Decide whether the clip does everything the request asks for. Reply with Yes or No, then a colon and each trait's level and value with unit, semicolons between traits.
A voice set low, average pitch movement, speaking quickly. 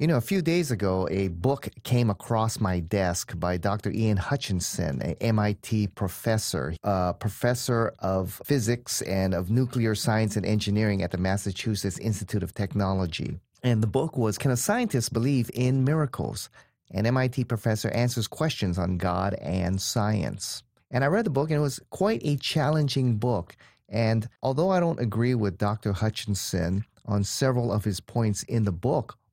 No: low, 110 Hz; average, 4.1 semitones; average, 170 wpm